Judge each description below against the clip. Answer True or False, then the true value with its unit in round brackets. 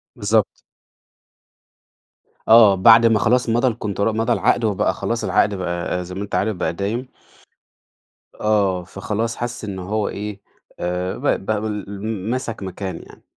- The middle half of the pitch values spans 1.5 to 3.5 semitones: True (3.0 semitones)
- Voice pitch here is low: True (105 Hz)